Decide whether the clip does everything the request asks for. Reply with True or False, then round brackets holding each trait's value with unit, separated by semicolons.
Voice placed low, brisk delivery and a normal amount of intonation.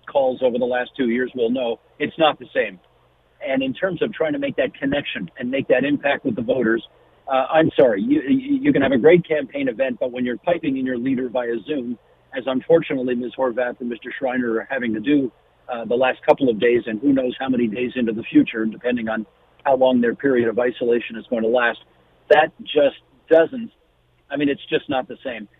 False (130 Hz; 225 wpm; 6.8 semitones)